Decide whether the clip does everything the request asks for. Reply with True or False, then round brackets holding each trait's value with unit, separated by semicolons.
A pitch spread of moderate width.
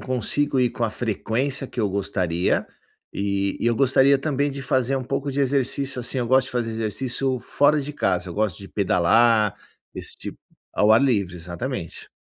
True (4.9 semitones)